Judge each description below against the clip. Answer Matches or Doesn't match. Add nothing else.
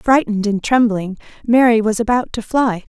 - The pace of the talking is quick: Doesn't match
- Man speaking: Doesn't match